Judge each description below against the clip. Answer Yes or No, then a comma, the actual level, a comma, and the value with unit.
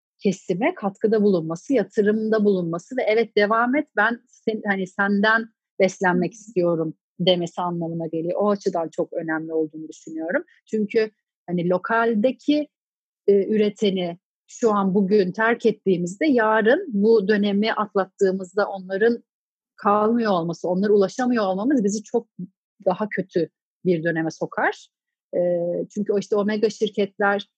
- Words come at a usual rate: Yes, average, 125 wpm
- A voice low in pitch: No, high, 205 Hz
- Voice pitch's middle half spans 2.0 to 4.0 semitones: Yes, average, 3.4 semitones